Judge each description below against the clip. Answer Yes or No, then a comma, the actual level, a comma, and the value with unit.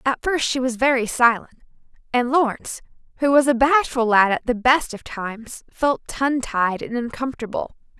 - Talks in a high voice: Yes, very high, 250 Hz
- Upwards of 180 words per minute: No, average, 175 wpm